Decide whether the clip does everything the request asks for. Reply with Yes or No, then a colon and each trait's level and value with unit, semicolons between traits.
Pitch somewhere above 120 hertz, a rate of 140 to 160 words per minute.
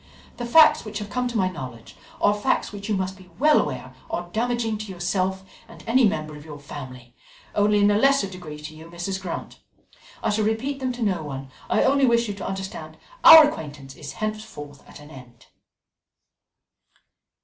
No: high, 190 Hz; average, 190 wpm